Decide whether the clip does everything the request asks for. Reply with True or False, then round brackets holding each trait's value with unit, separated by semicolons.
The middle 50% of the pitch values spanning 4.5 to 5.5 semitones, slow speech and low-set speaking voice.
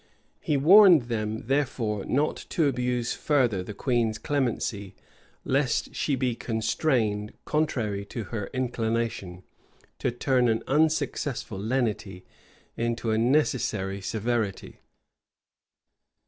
False (3.9 semitones; 105 wpm; 120 Hz)